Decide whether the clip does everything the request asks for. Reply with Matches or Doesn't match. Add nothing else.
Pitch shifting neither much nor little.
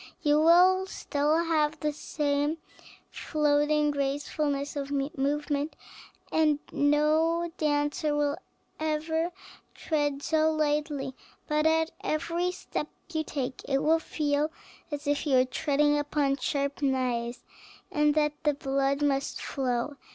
Doesn't match